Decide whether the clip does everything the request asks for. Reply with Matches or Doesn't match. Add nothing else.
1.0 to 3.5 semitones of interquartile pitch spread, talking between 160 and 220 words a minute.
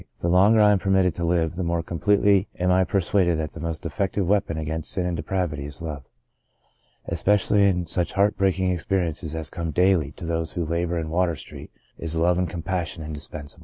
Matches